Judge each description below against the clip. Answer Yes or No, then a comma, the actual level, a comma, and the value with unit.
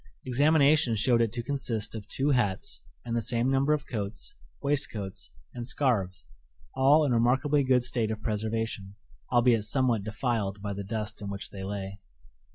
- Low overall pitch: Yes, low, 115 Hz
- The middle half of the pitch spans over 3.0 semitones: Yes, average, 4.3 semitones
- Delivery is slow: No, average, 165 wpm